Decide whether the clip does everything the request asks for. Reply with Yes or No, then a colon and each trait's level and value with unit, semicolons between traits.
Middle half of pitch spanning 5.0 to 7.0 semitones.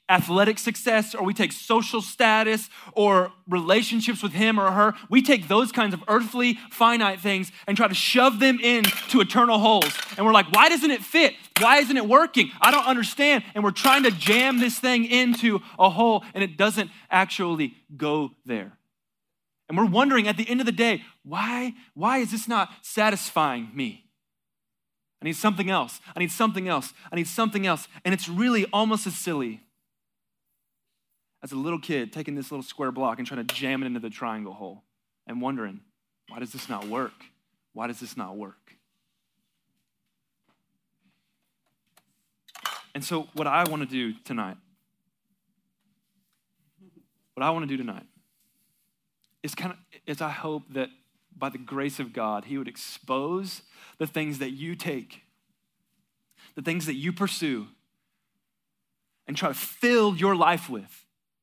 Yes: wide, 5.4 semitones